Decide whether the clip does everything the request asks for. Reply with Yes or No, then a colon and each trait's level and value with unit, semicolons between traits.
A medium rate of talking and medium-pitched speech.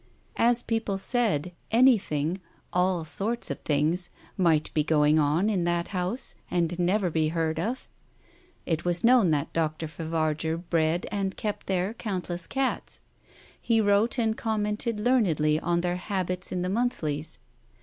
Yes: average, 150 wpm; medium, 180 Hz